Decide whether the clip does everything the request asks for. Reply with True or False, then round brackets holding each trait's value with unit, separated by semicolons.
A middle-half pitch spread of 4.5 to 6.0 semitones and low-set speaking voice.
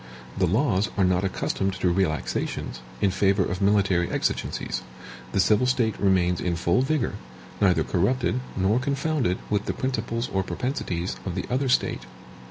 True (5.1 semitones; 95 Hz)